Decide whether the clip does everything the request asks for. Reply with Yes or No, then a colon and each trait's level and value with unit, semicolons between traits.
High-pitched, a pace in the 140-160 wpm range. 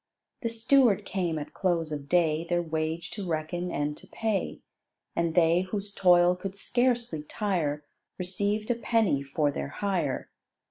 No: medium, 175 Hz; average, 150 wpm